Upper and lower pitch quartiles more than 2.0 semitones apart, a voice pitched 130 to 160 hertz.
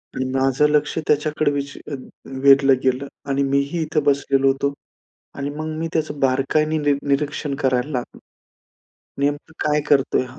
No: narrow, 1.7 semitones; medium, 140 Hz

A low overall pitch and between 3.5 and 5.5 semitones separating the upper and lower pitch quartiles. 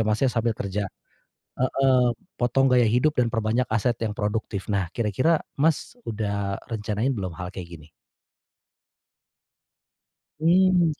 Yes: low, 115 Hz; average, 4.1 semitones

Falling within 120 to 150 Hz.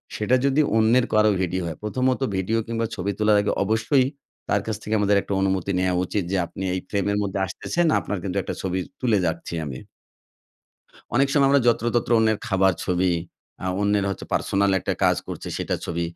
No: low, 105 Hz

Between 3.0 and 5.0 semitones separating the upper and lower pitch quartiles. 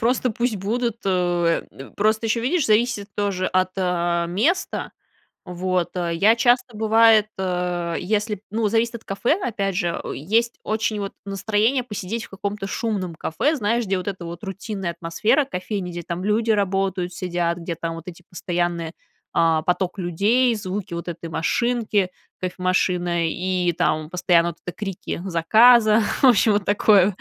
Yes: average, 3.9 semitones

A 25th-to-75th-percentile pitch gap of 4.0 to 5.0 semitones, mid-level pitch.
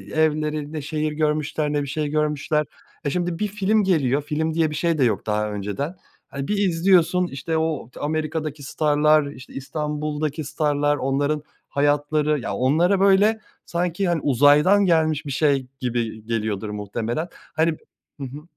No: narrow, 2.5 semitones; medium, 150 Hz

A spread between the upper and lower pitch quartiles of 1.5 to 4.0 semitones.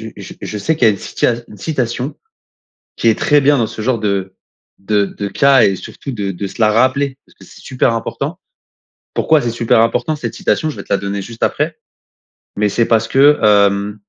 No: average, 4.9 semitones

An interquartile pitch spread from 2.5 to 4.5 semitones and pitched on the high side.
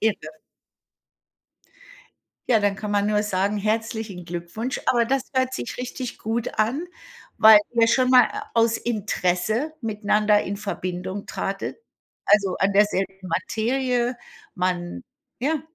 Yes: average, 3.4 semitones; high, 215 Hz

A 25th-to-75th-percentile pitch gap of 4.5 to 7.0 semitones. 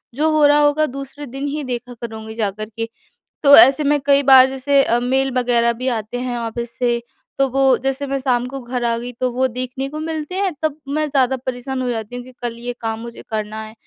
No: average, 2.8 semitones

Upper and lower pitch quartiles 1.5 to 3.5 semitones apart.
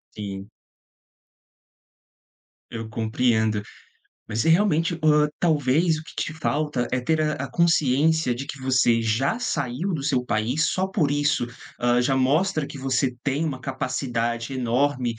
No: average, 4.2 semitones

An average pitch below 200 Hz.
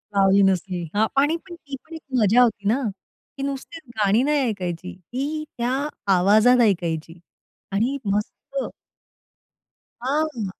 No: high, 225 Hz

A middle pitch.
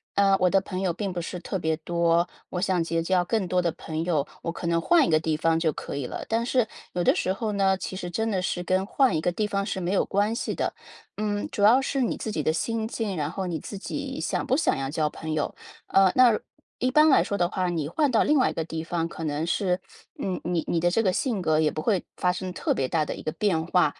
Yes: medium, 180 Hz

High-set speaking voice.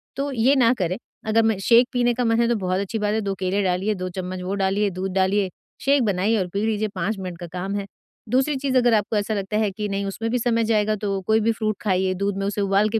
Yes: high, 205 Hz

